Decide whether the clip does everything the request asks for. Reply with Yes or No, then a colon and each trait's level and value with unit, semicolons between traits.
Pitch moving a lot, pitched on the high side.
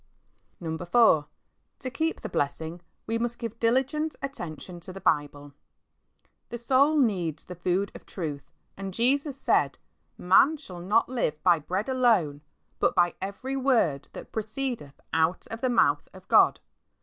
Yes: wide, 7.3 semitones; high, 200 Hz